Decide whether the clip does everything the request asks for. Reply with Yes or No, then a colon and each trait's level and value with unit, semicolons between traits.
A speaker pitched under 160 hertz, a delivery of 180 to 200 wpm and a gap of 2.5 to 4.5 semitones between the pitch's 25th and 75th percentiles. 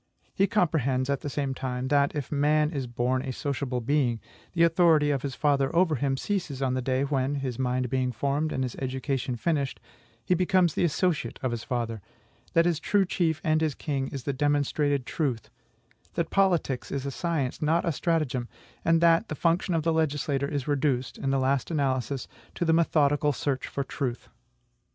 Yes: medium, 140 Hz; average, 190 wpm; average, 3.5 semitones